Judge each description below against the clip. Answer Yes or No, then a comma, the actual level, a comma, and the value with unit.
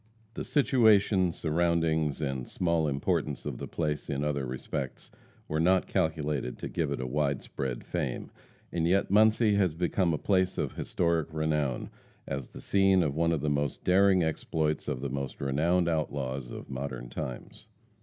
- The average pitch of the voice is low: Yes, very low, 80 Hz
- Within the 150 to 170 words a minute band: Yes, average, 165 wpm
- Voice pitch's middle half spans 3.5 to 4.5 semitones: Yes, average, 4.2 semitones